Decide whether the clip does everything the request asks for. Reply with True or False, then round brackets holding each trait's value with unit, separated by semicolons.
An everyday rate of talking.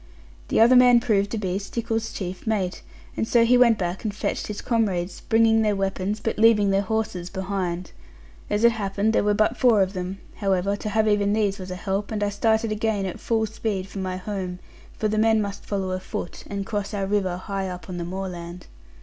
False (215 wpm)